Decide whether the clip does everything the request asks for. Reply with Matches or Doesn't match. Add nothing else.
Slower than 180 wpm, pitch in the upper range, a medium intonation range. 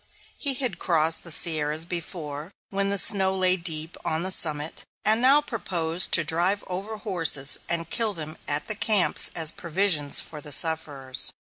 Doesn't match